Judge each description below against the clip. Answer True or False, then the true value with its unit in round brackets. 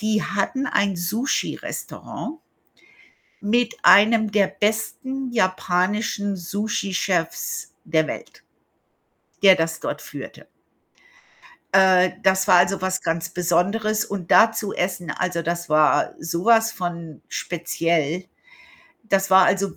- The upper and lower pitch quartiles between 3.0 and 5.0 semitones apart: True (3.5 semitones)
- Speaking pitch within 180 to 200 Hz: True (190 Hz)